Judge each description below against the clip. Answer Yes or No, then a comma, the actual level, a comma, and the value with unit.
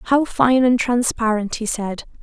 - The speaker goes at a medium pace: Yes, average, 160 wpm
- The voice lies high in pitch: Yes, high, 235 Hz